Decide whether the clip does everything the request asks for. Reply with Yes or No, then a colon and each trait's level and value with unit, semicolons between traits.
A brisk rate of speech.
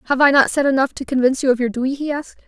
Yes: fast, 315 wpm